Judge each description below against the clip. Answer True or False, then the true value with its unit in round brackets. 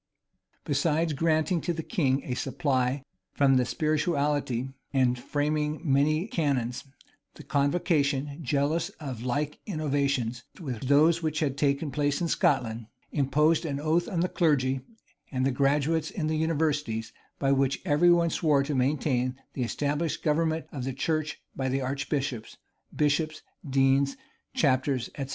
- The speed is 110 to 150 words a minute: True (140 wpm)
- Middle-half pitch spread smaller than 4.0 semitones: True (2.7 semitones)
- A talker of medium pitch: True (145 Hz)